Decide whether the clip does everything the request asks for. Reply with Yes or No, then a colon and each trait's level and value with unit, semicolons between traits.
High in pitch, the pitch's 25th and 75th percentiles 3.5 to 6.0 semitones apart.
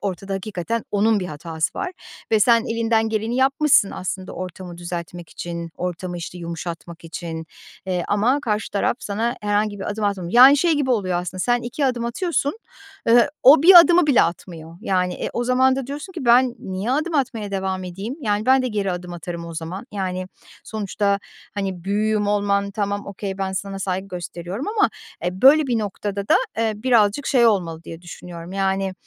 Yes: high, 200 Hz; average, 4.7 semitones